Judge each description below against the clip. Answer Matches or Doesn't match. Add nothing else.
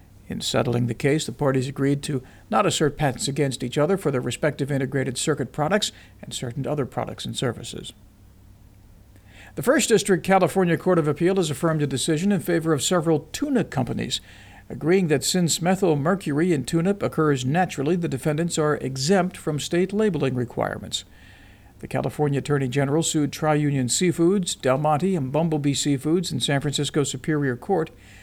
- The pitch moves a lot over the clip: Doesn't match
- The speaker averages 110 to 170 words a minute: Matches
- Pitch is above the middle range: Doesn't match